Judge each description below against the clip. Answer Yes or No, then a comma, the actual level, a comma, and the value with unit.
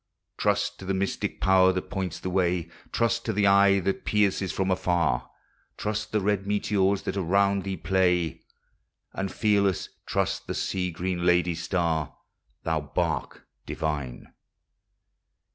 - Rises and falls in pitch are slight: Yes, narrow, 2.3 semitones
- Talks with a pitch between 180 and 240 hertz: No, very low, 95 Hz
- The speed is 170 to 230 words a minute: No, average, 140 wpm